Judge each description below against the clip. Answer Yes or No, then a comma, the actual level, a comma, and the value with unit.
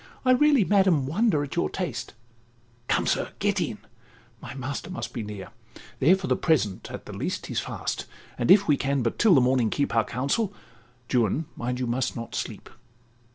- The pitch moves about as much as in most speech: No, wide, 7.2 semitones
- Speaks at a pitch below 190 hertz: Yes, low, 135 Hz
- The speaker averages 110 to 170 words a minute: No, average, 180 wpm